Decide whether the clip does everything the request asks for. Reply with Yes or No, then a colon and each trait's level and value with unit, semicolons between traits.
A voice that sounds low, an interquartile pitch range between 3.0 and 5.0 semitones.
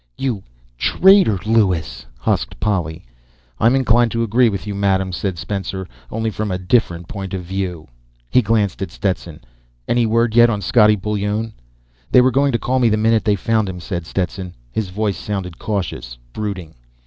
Yes: low, 105 Hz; average, 3.5 semitones